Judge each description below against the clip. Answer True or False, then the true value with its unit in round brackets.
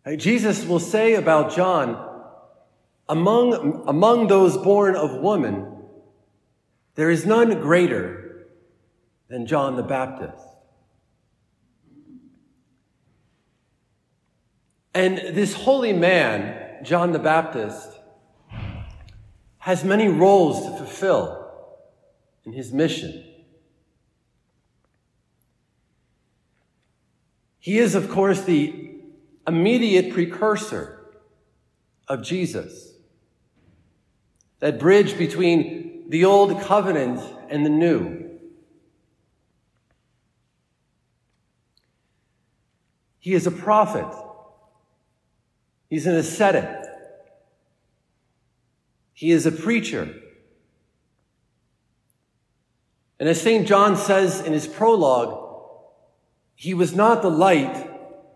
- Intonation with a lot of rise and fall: False (5.0 semitones)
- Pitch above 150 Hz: True (185 Hz)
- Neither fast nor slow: False (80 wpm)